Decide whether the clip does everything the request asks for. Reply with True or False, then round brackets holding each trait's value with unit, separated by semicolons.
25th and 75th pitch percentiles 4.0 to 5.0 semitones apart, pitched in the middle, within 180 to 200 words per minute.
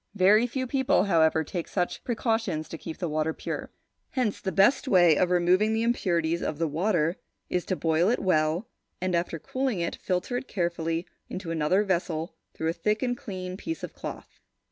True (4.5 semitones; 180 Hz; 190 wpm)